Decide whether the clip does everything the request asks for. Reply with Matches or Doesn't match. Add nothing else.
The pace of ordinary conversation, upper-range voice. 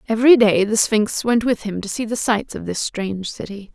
Doesn't match